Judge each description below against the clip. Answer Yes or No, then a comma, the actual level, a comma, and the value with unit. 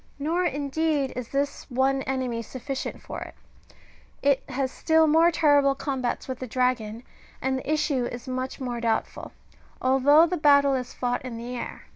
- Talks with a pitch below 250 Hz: No, very high, 265 Hz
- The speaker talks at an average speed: Yes, average, 165 wpm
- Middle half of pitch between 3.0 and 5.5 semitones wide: No, narrow, 2.4 semitones